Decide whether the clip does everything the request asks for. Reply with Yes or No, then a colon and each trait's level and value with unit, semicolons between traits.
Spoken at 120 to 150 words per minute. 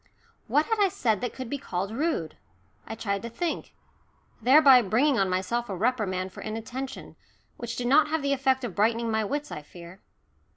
No: average, 190 wpm